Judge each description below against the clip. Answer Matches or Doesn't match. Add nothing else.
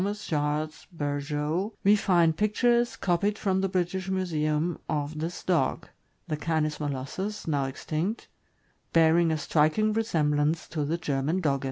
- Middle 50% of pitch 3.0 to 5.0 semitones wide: Matches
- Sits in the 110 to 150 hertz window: Doesn't match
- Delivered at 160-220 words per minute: Doesn't match